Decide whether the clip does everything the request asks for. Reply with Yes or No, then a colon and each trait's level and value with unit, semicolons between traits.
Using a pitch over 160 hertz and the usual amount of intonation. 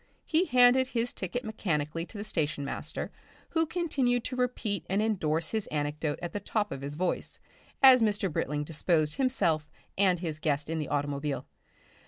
No: medium, 185 Hz; wide, 8.2 semitones